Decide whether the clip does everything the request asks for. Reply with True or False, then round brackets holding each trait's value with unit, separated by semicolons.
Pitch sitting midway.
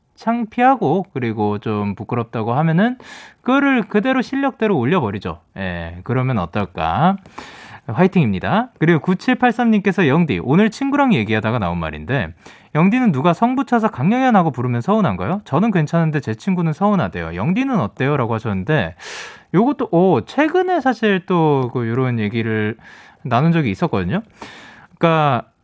True (170 Hz)